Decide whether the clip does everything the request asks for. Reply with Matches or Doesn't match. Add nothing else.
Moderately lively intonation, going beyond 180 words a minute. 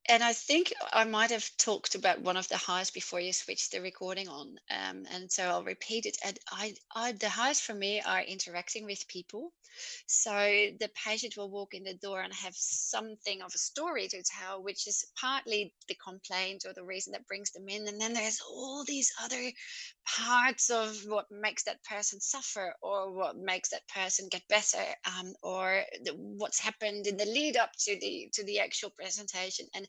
Matches